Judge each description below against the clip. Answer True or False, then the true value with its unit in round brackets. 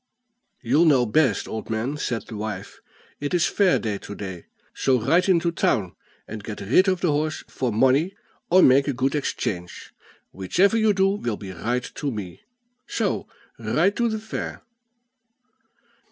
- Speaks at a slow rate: False (165 wpm)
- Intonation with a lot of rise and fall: True (8.2 semitones)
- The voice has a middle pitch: False (130 Hz)